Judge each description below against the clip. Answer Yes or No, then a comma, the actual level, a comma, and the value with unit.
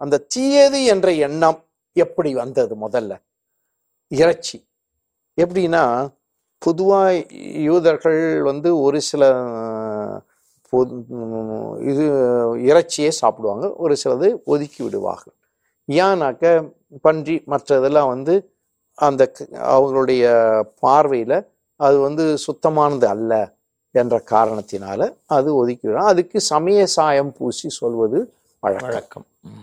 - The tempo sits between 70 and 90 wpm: Yes, average, 85 wpm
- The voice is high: No, medium, 150 Hz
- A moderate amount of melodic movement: Yes, average, 5.0 semitones